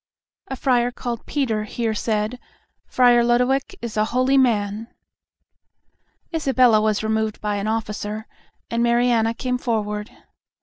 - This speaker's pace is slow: Yes, slow, 125 wpm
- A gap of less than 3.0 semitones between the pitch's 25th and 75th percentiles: Yes, narrow, 2.6 semitones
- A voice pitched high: Yes, high, 230 Hz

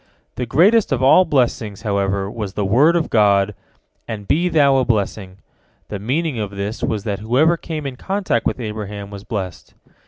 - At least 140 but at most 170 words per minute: No, average, 180 wpm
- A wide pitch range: Yes, wide, 6.0 semitones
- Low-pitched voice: Yes, low, 110 Hz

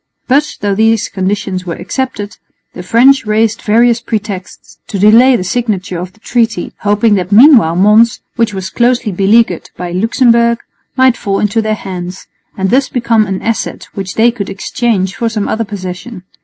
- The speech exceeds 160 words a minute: Yes, average, 170 wpm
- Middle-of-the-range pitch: No, high, 215 Hz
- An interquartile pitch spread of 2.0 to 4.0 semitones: Yes, average, 3.5 semitones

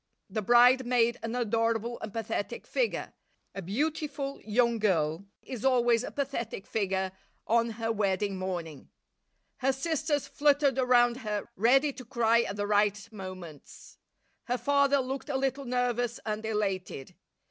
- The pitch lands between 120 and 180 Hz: No, high, 235 Hz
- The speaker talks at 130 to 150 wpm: Yes, average, 140 wpm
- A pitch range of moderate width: Yes, average, 4.1 semitones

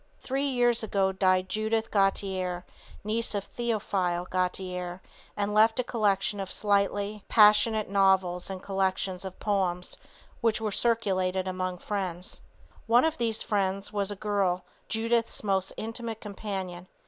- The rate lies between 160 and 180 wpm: No, slow, 135 wpm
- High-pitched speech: Yes, high, 200 Hz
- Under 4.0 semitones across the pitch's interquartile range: Yes, average, 2.8 semitones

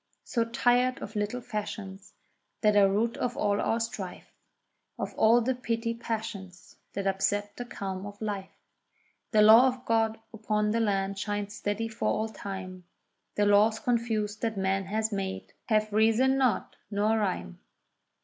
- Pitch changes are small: Yes, narrow, 2.2 semitones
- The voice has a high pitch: Yes, high, 215 Hz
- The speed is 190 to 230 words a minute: No, average, 155 wpm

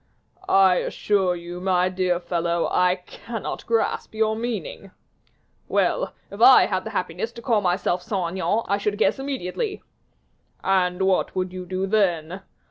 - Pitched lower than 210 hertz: Yes, high, 190 Hz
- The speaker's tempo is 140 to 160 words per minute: Yes, average, 150 wpm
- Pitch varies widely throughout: No, average, 3.2 semitones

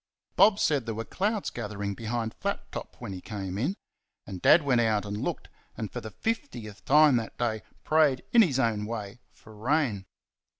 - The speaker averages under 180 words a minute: No, average, 185 wpm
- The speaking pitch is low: Yes, low, 115 Hz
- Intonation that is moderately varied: No, wide, 5.8 semitones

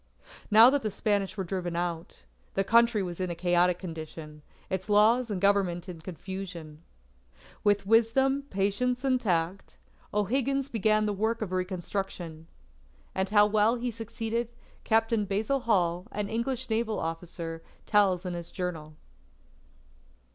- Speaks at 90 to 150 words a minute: Yes, average, 140 wpm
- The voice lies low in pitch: No, high, 200 Hz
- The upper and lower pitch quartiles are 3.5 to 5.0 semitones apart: Yes, average, 4.2 semitones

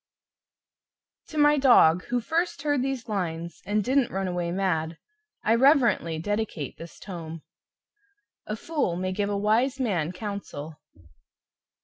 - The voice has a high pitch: Yes, high, 205 Hz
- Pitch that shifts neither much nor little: No, wide, 7.0 semitones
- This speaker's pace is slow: Yes, slow, 130 wpm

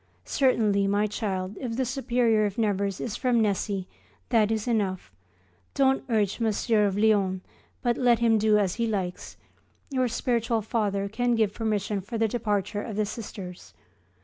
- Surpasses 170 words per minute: No, average, 160 wpm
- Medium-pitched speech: No, high, 215 Hz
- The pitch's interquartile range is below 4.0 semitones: Yes, narrow, 2.6 semitones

